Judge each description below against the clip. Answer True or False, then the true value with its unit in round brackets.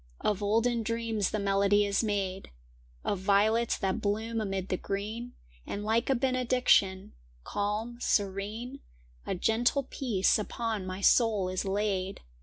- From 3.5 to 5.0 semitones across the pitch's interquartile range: False (2.7 semitones)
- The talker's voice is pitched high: True (210 Hz)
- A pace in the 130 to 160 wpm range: True (135 wpm)